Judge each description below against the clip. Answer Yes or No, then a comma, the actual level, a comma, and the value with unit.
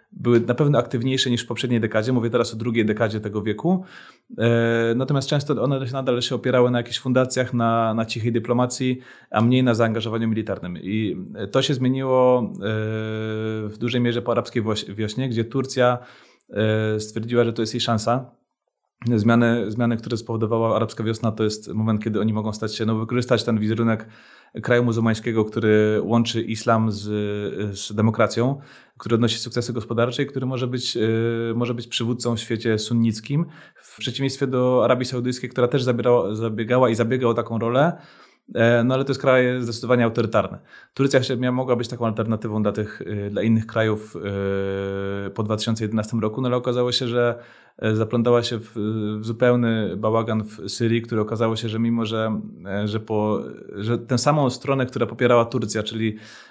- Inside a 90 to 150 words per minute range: No, fast, 160 wpm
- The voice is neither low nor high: No, low, 115 Hz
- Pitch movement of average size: No, narrow, 2.1 semitones